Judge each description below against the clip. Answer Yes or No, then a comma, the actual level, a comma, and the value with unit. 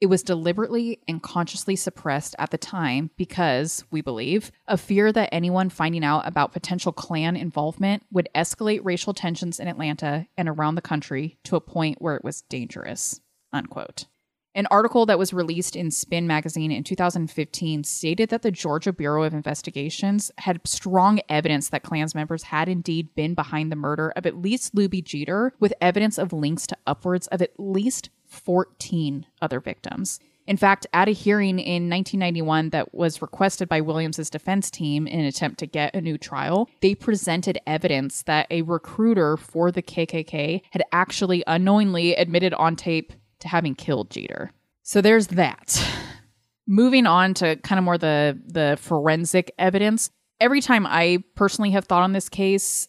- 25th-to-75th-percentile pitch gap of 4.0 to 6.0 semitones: No, average, 3.6 semitones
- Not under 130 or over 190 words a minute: Yes, average, 170 wpm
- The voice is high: No, medium, 175 Hz